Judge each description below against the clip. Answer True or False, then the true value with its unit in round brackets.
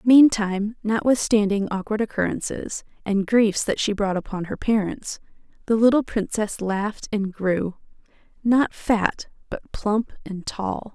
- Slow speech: True (125 wpm)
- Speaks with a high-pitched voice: True (210 Hz)